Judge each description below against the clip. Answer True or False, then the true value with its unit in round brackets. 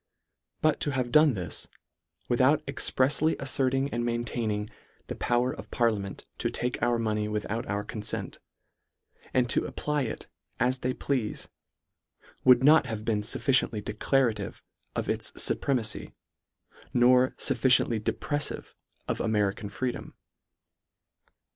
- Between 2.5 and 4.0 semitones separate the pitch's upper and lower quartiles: True (3.5 semitones)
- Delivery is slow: True (125 wpm)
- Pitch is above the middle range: False (120 Hz)